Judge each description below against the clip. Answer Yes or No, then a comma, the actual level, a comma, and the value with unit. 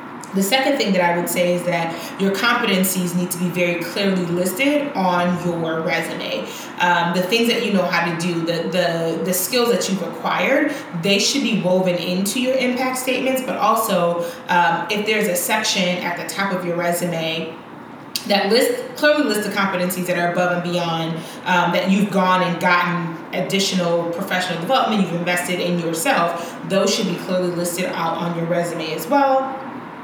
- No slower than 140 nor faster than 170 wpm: No, average, 185 wpm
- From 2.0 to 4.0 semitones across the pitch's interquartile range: Yes, average, 3.4 semitones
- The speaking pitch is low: No, medium, 180 Hz